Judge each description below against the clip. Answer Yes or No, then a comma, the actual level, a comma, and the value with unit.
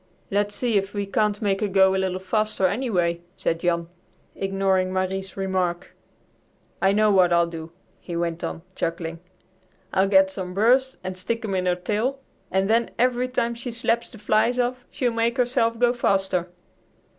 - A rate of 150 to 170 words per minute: No, average, 180 wpm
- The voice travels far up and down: No, average, 3.8 semitones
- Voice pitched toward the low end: No, high, 195 Hz